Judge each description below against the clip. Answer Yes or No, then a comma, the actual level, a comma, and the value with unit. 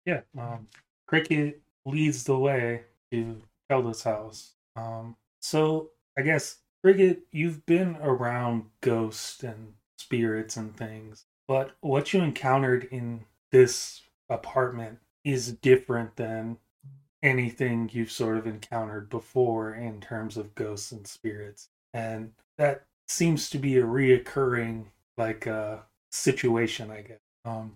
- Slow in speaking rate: Yes, slow, 125 wpm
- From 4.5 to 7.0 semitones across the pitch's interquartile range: No, average, 3.3 semitones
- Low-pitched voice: Yes, low, 115 Hz